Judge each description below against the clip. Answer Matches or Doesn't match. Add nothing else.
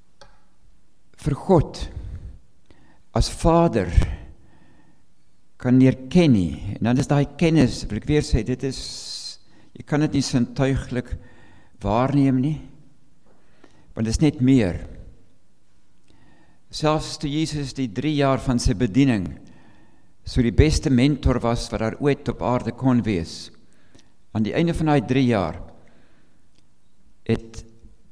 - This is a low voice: Matches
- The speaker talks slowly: Matches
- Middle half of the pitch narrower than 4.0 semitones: Doesn't match